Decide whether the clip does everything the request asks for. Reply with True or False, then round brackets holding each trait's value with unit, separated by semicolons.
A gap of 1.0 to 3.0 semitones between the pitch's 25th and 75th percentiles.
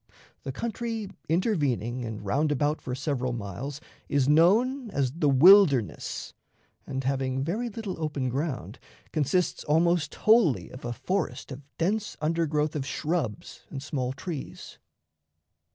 False (5.2 semitones)